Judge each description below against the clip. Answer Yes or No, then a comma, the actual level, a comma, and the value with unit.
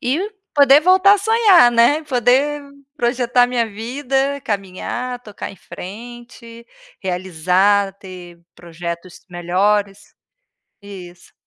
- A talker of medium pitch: No, high, 230 Hz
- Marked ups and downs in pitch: Yes, wide, 5.8 semitones